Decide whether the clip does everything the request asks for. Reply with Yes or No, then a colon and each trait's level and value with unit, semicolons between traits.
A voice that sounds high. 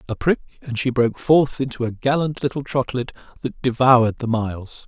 No: low, 125 Hz